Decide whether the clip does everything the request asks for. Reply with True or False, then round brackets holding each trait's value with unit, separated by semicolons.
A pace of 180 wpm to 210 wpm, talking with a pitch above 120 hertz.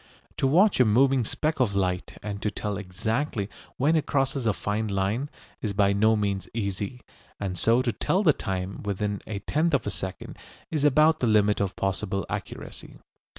False (185 wpm; 105 Hz)